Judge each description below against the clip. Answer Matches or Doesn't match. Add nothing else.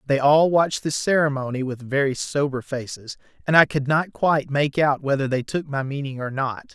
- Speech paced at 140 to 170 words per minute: Doesn't match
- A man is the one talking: Matches